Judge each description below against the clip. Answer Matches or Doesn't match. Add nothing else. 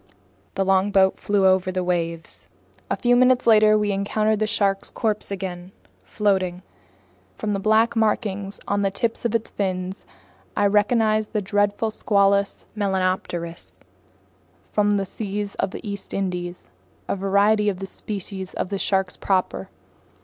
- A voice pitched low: Doesn't match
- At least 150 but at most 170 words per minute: Doesn't match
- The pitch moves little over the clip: Matches